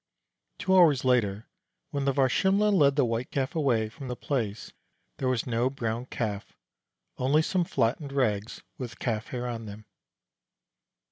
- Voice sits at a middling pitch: No, low, 125 Hz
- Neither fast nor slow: Yes, average, 150 wpm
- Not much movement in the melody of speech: No, average, 3.7 semitones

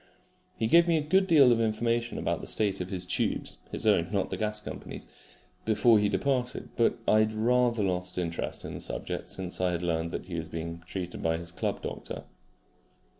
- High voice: No, low, 105 Hz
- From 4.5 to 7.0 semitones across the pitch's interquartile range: Yes, average, 4.8 semitones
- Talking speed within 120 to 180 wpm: No, fast, 205 wpm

